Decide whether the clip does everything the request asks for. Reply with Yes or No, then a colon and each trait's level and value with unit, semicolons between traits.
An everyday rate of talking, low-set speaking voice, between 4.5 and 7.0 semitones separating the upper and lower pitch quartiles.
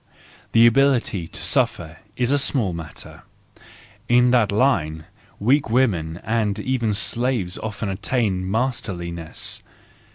No: slow, 110 wpm; low, 110 Hz; wide, 5.5 semitones